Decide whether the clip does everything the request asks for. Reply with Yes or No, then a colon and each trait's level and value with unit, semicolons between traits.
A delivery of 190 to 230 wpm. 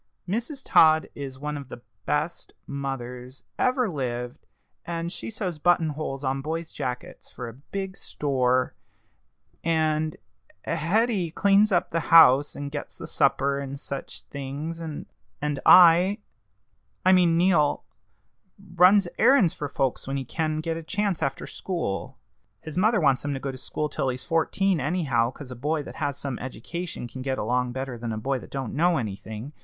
No: average, 165 wpm